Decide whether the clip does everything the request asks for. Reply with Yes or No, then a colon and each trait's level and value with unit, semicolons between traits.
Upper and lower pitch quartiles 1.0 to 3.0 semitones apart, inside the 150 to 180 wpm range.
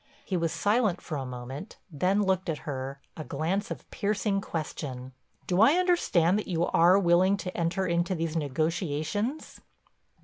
No: average, 4.1 semitones; average, 160 wpm